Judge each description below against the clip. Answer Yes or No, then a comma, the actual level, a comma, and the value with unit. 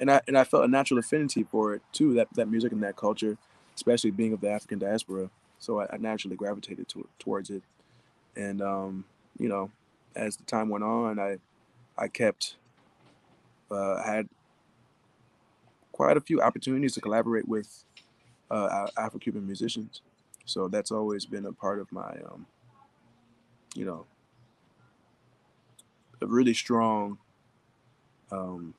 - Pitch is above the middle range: No, low, 110 Hz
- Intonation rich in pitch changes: No, narrow, 2.6 semitones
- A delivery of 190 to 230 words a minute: No, average, 150 wpm